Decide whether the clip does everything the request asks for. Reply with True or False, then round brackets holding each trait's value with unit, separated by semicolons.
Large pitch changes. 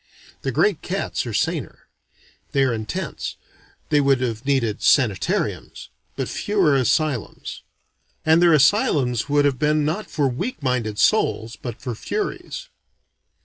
False (4.1 semitones)